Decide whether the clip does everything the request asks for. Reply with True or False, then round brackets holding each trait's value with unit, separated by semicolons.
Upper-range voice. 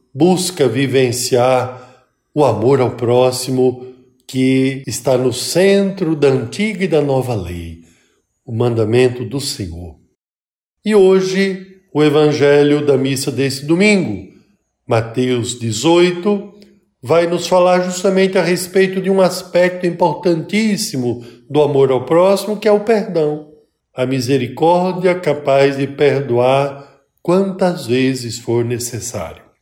False (140 Hz)